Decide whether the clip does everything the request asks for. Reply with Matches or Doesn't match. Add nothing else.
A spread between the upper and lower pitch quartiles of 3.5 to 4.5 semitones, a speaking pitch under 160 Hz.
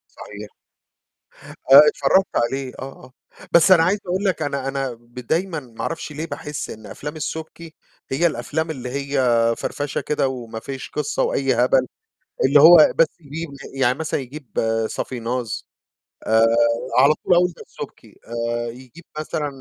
Matches